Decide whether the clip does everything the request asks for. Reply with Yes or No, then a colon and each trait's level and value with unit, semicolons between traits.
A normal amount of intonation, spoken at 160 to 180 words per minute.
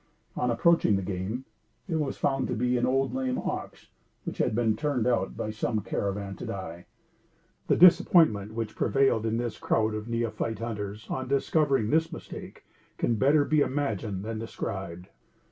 Yes: average, 4.1 semitones; average, 165 wpm